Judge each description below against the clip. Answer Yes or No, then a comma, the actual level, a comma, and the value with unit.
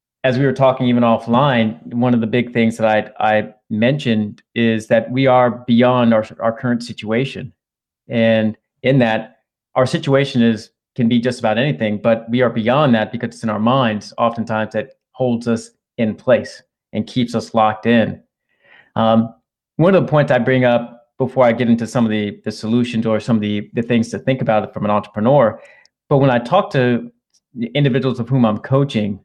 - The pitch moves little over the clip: Yes, narrow, 2.3 semitones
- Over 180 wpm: Yes, average, 200 wpm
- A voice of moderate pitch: No, low, 115 Hz